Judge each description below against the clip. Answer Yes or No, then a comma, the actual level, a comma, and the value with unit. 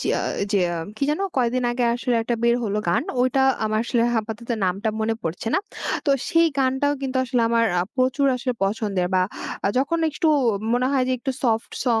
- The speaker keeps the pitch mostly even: No, average, 3.2 semitones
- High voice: Yes, high, 240 Hz